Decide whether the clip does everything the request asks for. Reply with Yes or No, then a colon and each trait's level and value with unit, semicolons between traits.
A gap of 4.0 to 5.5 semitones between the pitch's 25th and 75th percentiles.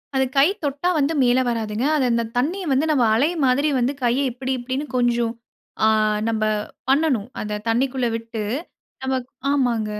No: average, 3.0 semitones